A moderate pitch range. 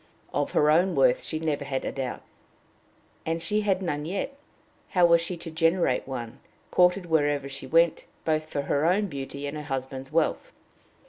Yes: average, 3.8 semitones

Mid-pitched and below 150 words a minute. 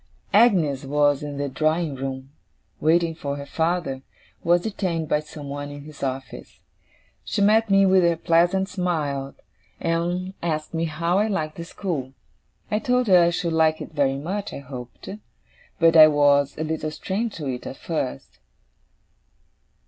No: medium, 160 Hz; average, 165 wpm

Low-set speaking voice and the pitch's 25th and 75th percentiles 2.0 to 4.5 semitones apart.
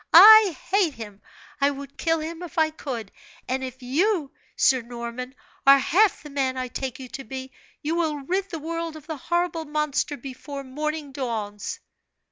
No: very high, 280 Hz; average, 3.9 semitones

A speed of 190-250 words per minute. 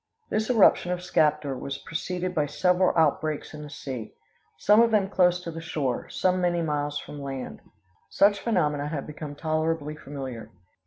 No: average, 165 wpm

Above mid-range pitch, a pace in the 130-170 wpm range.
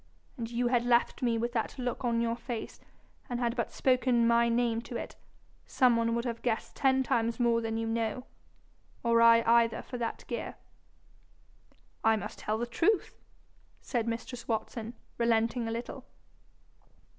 Yes: high, 235 Hz; average, 165 wpm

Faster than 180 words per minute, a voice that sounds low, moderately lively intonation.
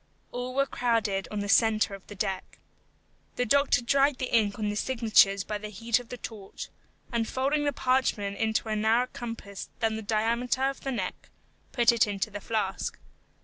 No: average, 190 wpm; high, 225 Hz; average, 3.2 semitones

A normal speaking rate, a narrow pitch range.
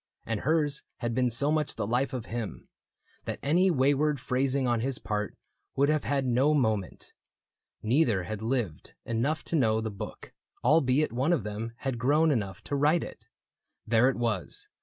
No: average, 175 wpm; average, 4.3 semitones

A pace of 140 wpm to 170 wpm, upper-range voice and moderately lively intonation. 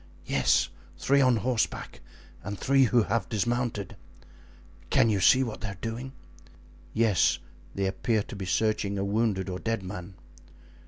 No: average, 150 wpm; low, 110 Hz; average, 3.3 semitones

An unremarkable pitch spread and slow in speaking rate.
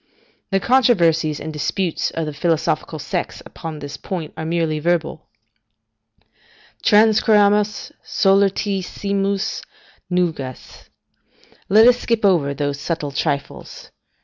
Yes: average, 4.5 semitones; slow, 100 wpm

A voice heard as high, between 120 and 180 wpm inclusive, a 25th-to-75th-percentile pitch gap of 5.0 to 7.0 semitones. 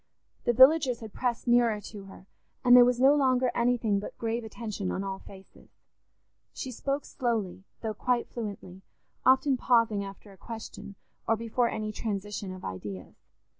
No: high, 225 Hz; average, 160 wpm; average, 3.7 semitones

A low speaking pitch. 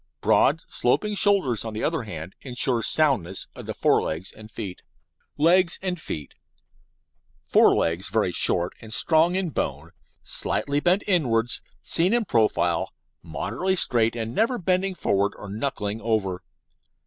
Yes: low, 115 Hz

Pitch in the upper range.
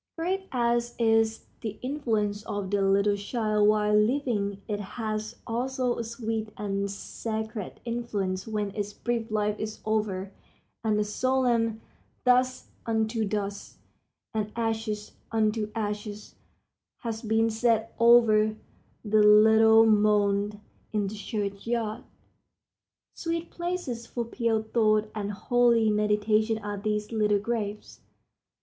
Yes: high, 215 Hz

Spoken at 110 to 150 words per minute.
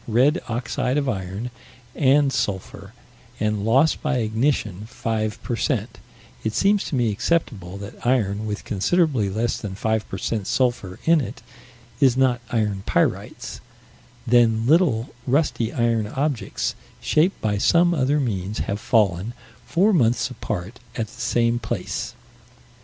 Yes: average, 140 wpm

